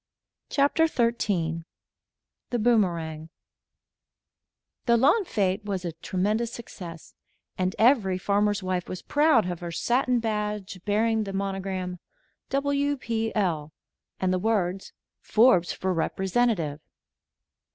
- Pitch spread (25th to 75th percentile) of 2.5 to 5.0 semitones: Yes, average, 4.3 semitones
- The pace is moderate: No, slow, 110 wpm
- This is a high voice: Yes, high, 200 Hz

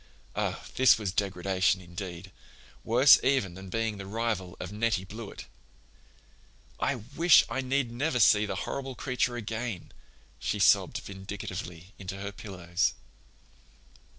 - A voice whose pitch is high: No, low, 105 Hz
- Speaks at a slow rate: Yes, slow, 125 wpm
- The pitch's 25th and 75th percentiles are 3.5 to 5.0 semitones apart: Yes, average, 4.2 semitones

